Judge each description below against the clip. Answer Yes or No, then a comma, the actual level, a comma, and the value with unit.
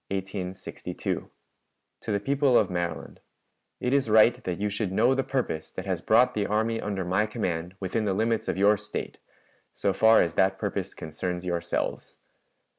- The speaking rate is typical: Yes, average, 170 wpm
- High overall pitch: No, low, 100 Hz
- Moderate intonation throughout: Yes, average, 3.5 semitones